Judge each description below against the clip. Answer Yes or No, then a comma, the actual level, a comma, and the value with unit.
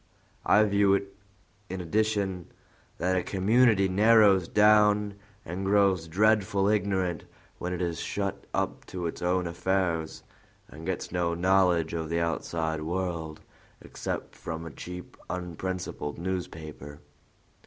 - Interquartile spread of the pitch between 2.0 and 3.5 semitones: Yes, average, 2.9 semitones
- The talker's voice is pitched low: Yes, very low, 90 Hz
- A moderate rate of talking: No, slow, 125 wpm